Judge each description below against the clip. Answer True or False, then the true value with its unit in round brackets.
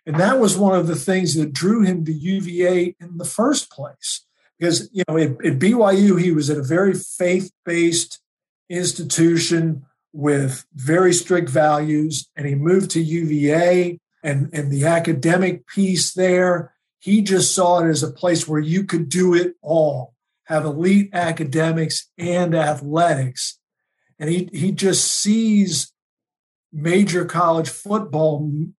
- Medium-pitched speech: True (170 Hz)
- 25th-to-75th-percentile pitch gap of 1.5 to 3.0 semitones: True (2.7 semitones)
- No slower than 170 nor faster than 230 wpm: False (150 wpm)